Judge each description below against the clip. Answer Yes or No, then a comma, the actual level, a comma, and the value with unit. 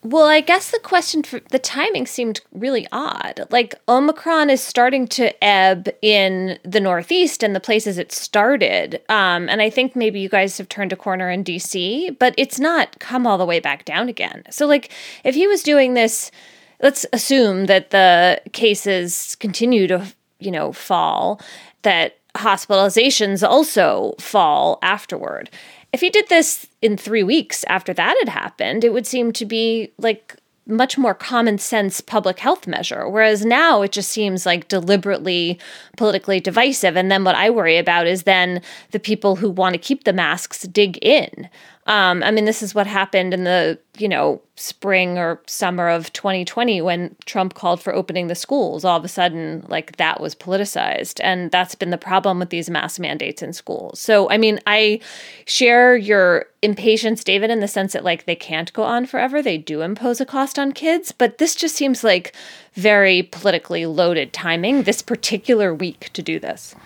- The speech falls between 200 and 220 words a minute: No, average, 180 wpm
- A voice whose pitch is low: No, high, 210 Hz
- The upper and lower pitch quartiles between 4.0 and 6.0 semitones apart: Yes, average, 4.7 semitones